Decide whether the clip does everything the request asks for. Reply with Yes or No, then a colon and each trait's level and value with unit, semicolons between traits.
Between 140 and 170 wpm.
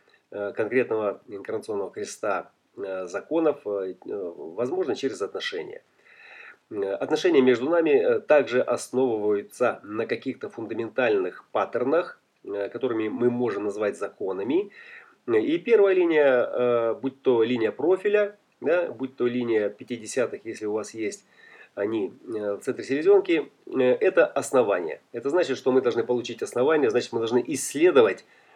No: average, 115 wpm